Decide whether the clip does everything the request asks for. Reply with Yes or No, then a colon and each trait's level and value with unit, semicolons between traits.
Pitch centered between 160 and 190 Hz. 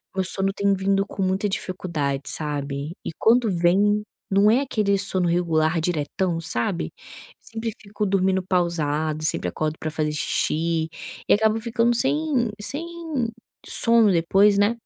Yes: medium, 185 Hz